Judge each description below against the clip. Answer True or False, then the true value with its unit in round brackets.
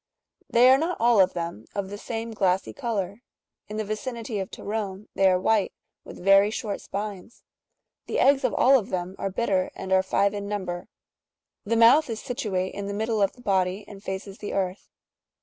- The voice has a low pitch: False (205 Hz)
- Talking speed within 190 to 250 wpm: True (195 wpm)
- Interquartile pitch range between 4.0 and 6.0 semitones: False (3.0 semitones)